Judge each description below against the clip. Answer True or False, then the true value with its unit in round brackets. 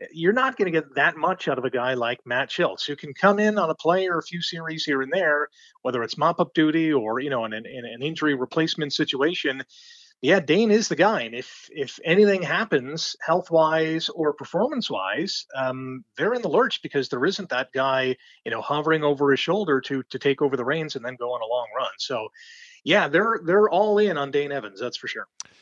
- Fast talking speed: True (220 wpm)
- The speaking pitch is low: False (155 Hz)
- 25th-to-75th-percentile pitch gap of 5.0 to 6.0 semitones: True (5.5 semitones)